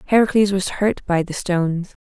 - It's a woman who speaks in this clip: Yes, female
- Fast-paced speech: No, average, 175 wpm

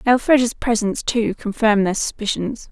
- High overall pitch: Yes, high, 220 Hz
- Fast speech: No, slow, 130 wpm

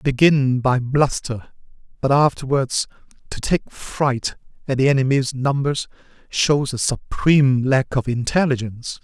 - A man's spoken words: Yes, male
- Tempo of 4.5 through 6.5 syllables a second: No, 4.3 syllables/s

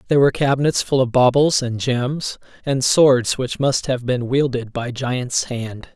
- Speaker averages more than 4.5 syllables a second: No, 4.4 syllables/s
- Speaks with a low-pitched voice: Yes, low, 130 Hz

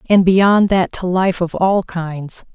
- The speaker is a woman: Yes, female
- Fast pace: No, average, 190 wpm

